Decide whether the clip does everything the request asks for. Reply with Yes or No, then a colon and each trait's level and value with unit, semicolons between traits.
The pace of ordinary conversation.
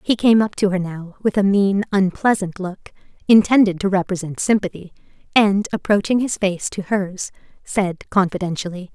Yes: average, 155 wpm